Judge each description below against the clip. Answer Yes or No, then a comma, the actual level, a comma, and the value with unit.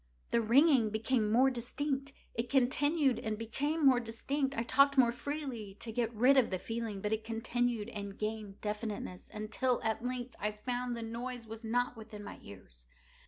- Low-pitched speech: No, high, 235 Hz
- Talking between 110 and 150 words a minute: No, average, 170 wpm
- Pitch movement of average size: Yes, average, 3.0 semitones